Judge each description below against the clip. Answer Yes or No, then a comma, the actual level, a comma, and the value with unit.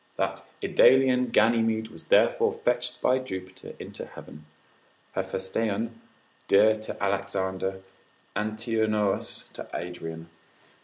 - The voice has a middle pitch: No, low, 110 Hz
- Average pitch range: Yes, average, 3.3 semitones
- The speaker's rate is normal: No, slow, 95 wpm